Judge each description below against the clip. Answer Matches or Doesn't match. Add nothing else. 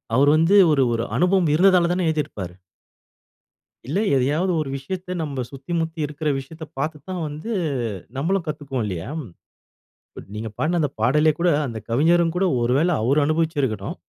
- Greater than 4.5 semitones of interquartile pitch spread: Doesn't match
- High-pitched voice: Doesn't match